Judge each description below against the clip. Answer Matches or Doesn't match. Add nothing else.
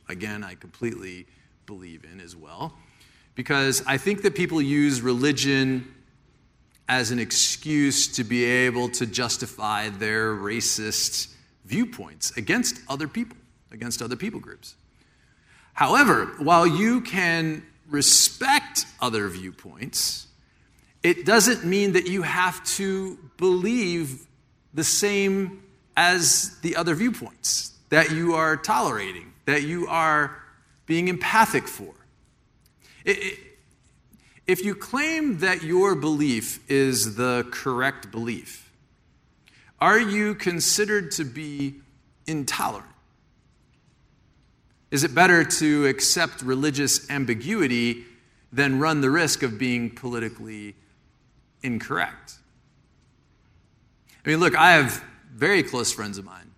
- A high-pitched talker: Doesn't match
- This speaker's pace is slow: Matches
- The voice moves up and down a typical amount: Doesn't match